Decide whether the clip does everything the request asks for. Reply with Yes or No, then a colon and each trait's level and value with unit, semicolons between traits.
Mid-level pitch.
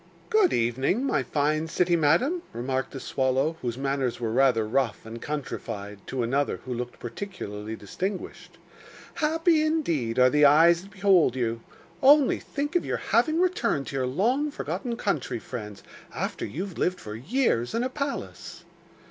Yes: medium, 145 Hz